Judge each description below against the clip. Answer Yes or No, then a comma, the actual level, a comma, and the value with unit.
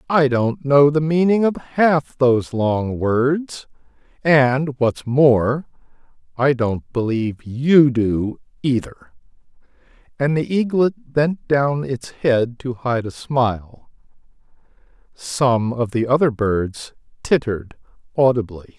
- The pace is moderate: No, slow, 120 wpm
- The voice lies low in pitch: Yes, low, 130 Hz